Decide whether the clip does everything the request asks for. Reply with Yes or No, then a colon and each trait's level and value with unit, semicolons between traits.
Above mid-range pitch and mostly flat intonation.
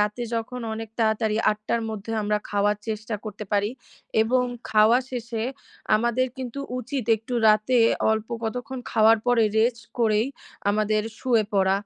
Yes: high, 220 Hz; narrow, 2.1 semitones